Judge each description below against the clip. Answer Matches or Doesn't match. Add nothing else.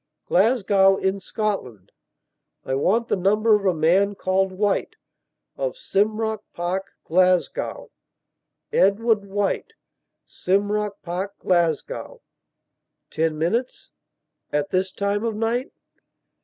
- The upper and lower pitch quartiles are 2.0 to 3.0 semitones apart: Matches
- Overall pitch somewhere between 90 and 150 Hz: Doesn't match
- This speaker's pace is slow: Matches